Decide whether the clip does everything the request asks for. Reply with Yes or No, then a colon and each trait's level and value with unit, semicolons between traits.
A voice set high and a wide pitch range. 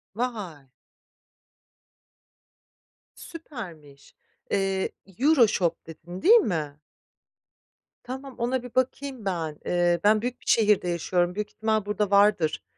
Yes: high, 205 Hz; wide, 5.8 semitones